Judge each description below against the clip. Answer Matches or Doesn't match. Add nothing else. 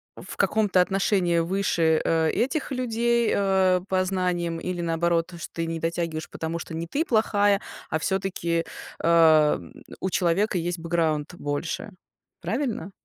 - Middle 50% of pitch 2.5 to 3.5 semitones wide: Matches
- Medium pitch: Matches